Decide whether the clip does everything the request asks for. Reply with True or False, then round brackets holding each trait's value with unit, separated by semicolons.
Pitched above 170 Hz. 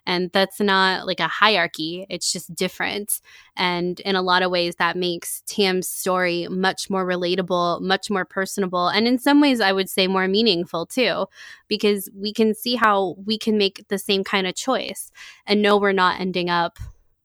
True (190 Hz)